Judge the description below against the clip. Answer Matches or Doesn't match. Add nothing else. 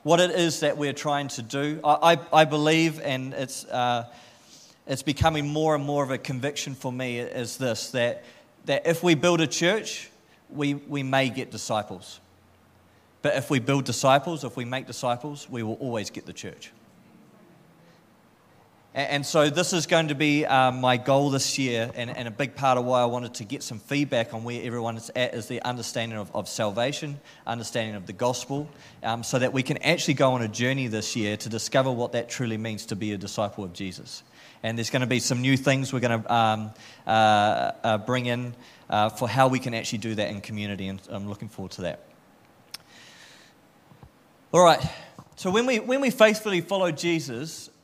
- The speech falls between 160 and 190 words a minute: Doesn't match